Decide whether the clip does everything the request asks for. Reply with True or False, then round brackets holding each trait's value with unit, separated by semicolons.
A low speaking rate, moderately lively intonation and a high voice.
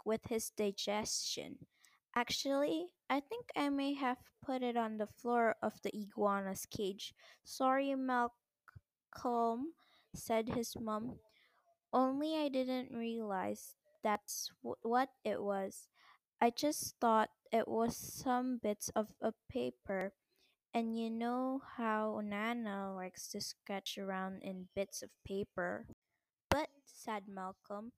True (125 wpm; 3.9 semitones; 230 Hz)